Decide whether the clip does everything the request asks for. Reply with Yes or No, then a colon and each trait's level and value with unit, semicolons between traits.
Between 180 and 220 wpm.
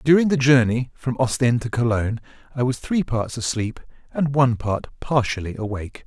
No: average, 170 wpm